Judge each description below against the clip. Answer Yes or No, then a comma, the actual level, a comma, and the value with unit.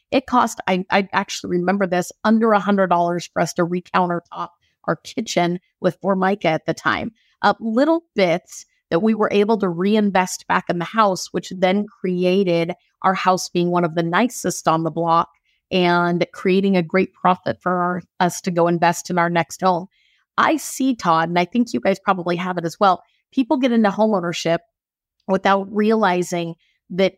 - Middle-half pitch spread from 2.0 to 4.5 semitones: Yes, average, 2.9 semitones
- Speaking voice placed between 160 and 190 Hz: Yes, medium, 185 Hz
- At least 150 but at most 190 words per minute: Yes, average, 180 wpm